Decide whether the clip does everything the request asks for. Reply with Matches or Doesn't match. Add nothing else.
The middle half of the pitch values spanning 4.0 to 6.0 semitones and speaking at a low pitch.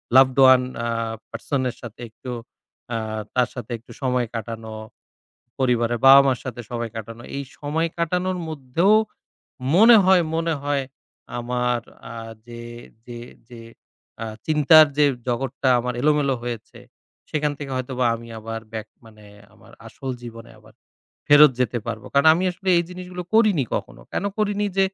Matches